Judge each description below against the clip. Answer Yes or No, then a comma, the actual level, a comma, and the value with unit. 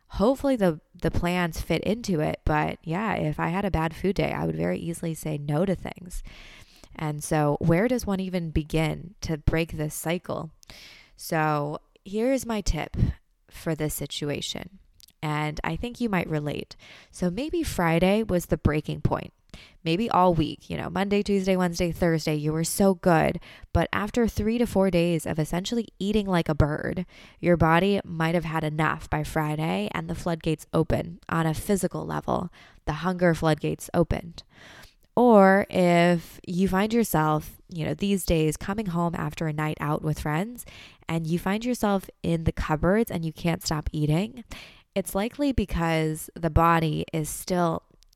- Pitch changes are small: No, average, 3.5 semitones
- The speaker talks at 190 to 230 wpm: No, average, 170 wpm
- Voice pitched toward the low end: No, medium, 170 Hz